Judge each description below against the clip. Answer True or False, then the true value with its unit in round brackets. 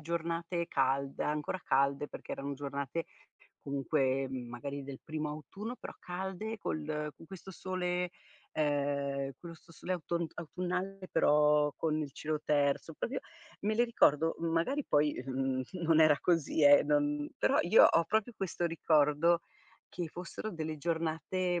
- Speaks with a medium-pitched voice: True (155 Hz)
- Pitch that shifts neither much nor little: True (3.4 semitones)